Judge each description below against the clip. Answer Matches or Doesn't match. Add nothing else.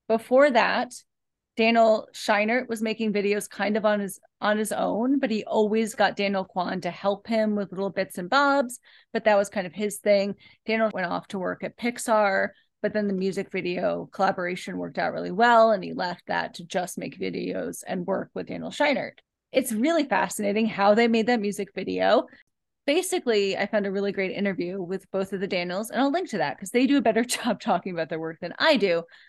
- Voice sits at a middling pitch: Doesn't match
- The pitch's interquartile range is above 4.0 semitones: Doesn't match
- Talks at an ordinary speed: Doesn't match